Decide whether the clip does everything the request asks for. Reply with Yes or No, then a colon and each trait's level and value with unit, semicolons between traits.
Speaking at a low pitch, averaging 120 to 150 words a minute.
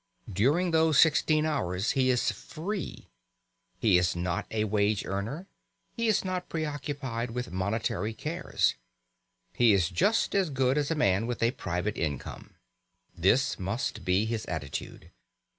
Yes: low, 115 Hz; average, 140 wpm